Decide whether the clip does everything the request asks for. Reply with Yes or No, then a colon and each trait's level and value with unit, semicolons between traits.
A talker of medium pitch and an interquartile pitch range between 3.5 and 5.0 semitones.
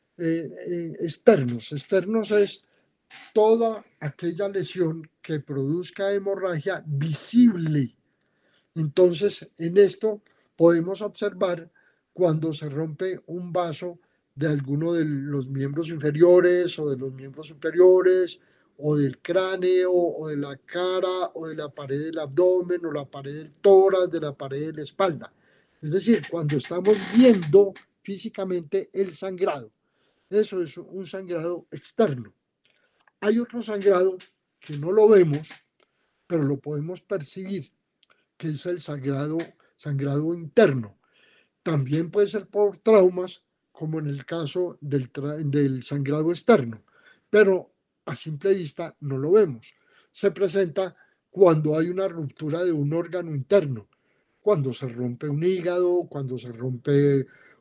Yes: medium, 170 Hz; average, 4.3 semitones